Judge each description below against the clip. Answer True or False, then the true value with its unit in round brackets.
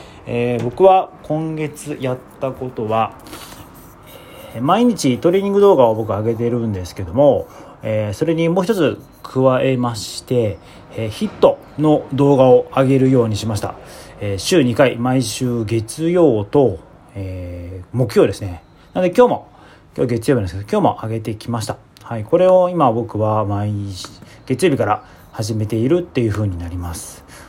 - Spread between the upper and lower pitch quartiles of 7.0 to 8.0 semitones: False (5.2 semitones)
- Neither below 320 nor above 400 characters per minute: False (305 characters per minute)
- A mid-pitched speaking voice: False (120 Hz)